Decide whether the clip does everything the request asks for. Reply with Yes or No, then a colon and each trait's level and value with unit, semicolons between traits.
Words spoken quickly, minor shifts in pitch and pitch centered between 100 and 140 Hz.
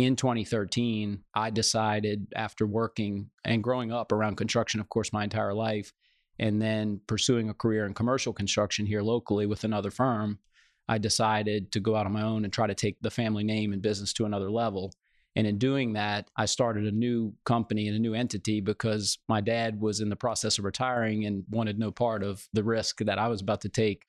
Yes: fast, 210 wpm; narrow, 1.5 semitones; low, 110 Hz